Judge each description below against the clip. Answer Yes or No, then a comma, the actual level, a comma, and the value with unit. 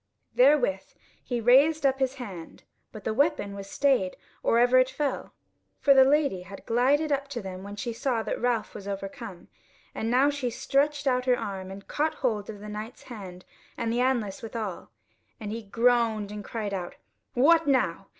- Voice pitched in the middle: No, high, 235 Hz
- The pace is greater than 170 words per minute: Yes, average, 185 wpm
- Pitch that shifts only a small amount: No, average, 5.0 semitones